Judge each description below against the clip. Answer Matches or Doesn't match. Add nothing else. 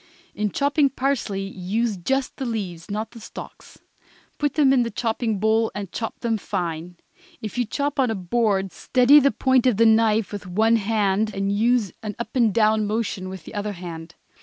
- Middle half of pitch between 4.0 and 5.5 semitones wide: Doesn't match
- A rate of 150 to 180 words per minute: Doesn't match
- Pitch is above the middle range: Matches